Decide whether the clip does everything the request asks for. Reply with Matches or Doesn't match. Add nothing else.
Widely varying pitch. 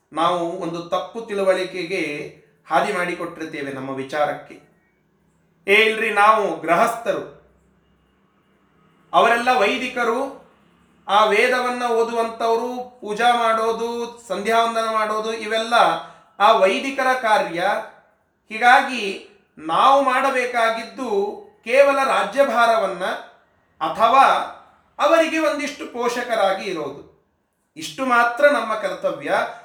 Doesn't match